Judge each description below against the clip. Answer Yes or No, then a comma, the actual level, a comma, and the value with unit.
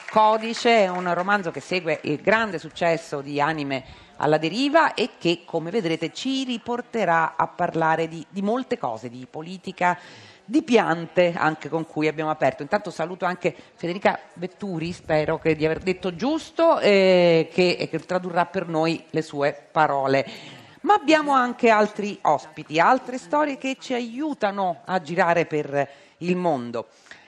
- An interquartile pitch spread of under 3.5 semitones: No, wide, 5.6 semitones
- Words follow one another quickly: No, average, 150 wpm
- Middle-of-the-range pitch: Yes, medium, 175 Hz